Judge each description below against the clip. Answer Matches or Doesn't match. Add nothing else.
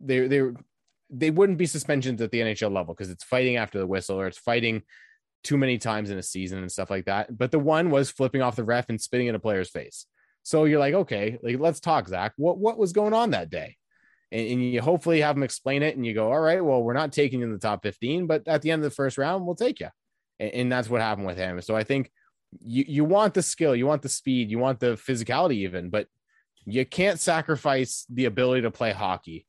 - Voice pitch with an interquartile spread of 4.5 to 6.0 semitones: Matches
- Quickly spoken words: Matches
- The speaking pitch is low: Matches